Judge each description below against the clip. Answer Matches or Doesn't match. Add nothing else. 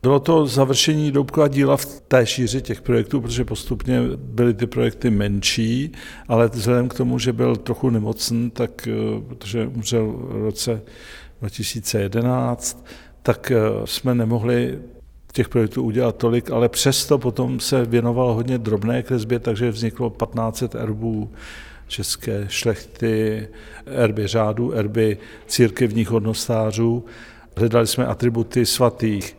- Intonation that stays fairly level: Matches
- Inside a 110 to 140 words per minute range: Matches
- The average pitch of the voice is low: Matches